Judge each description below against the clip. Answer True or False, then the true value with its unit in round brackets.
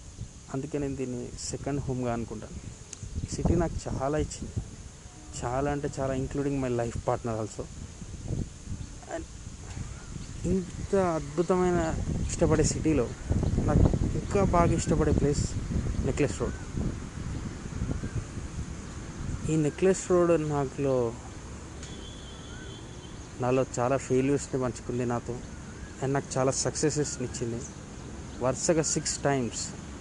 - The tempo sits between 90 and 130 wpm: True (95 wpm)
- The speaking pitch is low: True (125 Hz)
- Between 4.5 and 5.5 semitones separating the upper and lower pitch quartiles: False (4.1 semitones)